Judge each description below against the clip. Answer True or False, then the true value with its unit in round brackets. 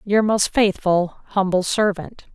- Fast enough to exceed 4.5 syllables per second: False (4.0 syllables/s)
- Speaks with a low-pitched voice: False (195 Hz)